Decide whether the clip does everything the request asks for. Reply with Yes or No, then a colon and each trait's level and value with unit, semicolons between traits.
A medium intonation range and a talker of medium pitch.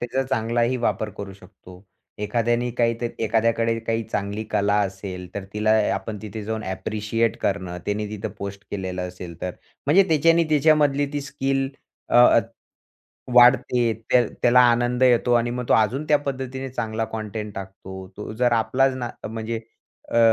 No: average, 3.3 semitones; low, 115 Hz